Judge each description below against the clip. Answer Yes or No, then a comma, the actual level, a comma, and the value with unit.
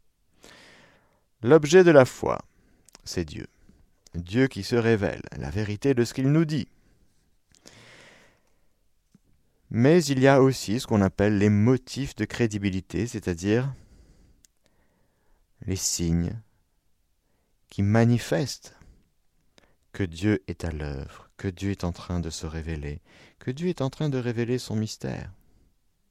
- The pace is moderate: No, slow, 130 wpm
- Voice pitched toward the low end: Yes, low, 105 Hz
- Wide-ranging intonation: Yes, wide, 6.0 semitones